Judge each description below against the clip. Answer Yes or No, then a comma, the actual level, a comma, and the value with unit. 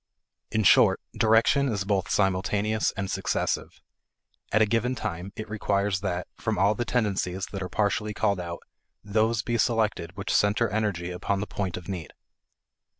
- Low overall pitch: Yes, low, 100 Hz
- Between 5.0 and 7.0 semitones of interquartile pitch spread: No, narrow, 2.4 semitones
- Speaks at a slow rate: No, average, 160 wpm